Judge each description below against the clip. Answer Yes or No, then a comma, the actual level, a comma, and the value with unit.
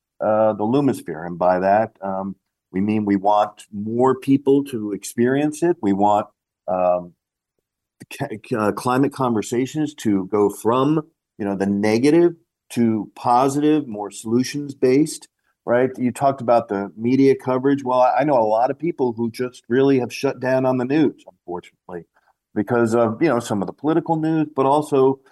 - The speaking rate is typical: Yes, average, 165 wpm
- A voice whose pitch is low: Yes, low, 125 Hz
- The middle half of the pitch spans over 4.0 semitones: Yes, average, 4.7 semitones